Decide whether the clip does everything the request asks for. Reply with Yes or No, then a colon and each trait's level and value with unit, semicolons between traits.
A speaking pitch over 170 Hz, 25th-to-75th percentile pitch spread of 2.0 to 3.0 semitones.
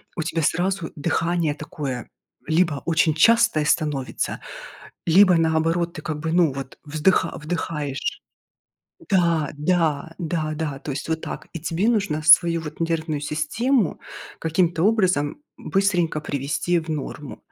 No: medium, 160 Hz; narrow, 2.6 semitones